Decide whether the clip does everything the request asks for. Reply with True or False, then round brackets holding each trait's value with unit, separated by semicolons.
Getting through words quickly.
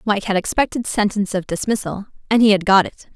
True (210 wpm)